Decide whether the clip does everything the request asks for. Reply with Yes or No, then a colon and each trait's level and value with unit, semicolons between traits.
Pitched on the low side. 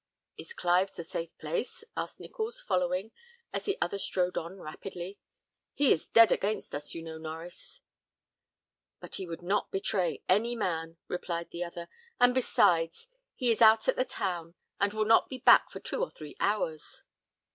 No: medium, 185 Hz